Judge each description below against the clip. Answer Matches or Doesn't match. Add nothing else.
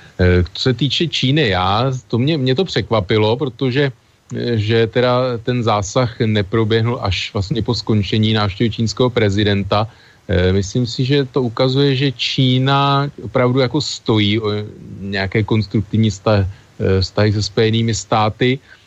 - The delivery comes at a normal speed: Matches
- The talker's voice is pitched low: Matches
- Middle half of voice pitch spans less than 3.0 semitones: Doesn't match